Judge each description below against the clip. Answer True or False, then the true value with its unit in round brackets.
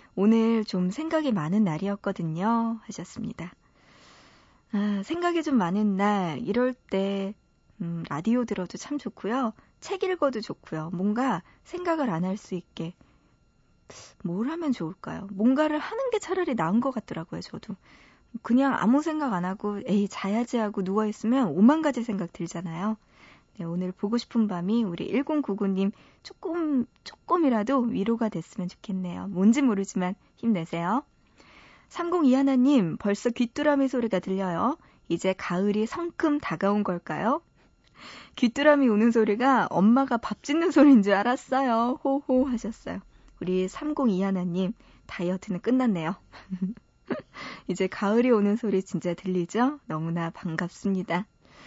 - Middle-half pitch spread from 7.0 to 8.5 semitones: False (5.6 semitones)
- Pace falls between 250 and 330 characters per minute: True (280 characters per minute)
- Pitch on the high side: True (215 Hz)